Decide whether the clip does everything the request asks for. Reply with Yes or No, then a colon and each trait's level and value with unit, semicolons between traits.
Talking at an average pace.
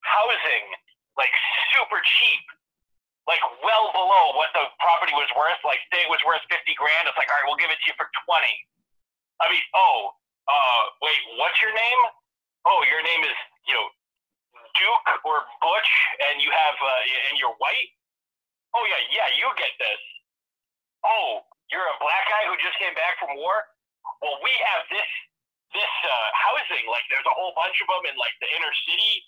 Yes: average, 180 wpm